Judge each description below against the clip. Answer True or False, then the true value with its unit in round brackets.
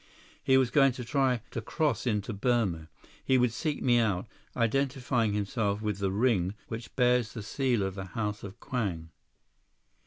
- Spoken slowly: False (165 wpm)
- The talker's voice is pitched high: False (115 Hz)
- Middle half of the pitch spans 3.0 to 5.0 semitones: True (3.8 semitones)